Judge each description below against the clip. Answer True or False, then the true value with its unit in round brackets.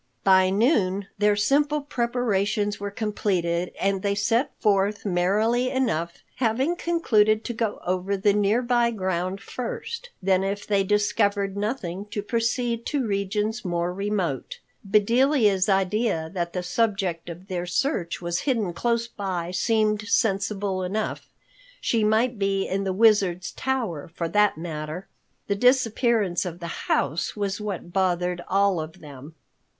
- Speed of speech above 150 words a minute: False (140 wpm)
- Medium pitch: False (200 Hz)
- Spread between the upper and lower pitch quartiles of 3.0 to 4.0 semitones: True (3.7 semitones)